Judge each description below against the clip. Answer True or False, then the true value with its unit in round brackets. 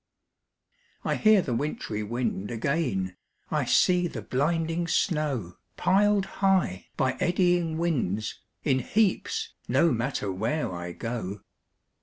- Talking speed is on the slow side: True (115 wpm)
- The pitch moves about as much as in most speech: False (8.1 semitones)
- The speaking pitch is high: False (145 Hz)